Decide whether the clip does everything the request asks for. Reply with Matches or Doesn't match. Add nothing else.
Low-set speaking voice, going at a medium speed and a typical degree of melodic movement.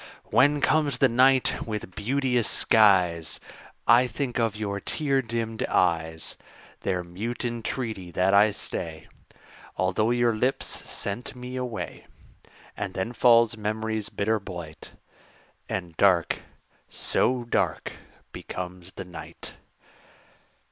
Doesn't match